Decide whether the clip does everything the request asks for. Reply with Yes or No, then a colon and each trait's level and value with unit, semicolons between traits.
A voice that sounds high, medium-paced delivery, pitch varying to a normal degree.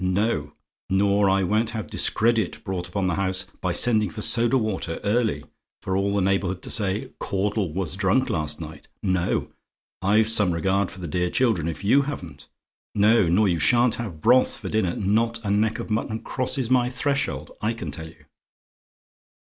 No: low, 100 Hz; average, 180 wpm; average, 3.4 semitones